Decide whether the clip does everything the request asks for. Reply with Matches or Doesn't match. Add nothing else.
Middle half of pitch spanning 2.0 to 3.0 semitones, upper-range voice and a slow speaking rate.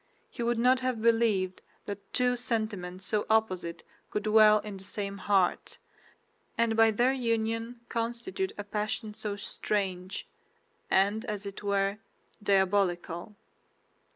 Matches